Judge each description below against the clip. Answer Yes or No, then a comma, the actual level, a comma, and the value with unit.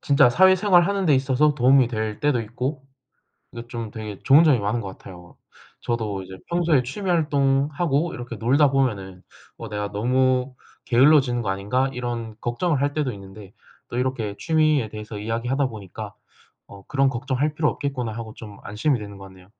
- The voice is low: Yes, low, 125 Hz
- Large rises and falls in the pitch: No, average, 4.9 semitones